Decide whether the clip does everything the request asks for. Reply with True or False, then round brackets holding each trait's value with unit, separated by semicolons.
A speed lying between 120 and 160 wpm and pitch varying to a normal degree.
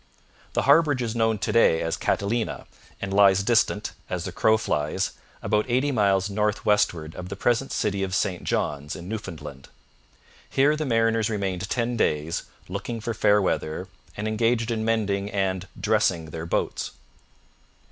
True (155 wpm; 3.3 semitones)